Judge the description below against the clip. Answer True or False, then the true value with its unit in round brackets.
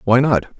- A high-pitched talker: False (125 Hz)